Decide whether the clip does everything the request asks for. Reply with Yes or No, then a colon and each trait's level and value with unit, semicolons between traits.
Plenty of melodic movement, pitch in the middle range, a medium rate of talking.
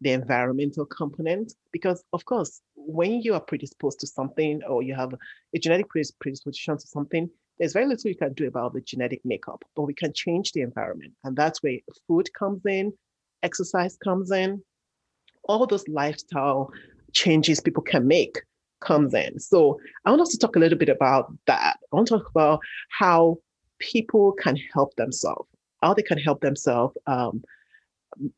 Yes: wide, 5.8 semitones; medium, 165 Hz; average, 175 wpm